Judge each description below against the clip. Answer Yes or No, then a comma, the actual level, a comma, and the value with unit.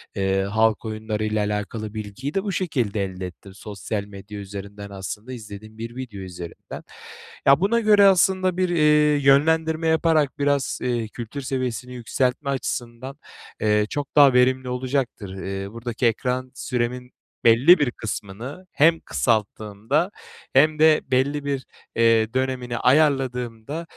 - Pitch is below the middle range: Yes, low, 125 Hz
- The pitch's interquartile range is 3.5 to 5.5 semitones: Yes, average, 5.1 semitones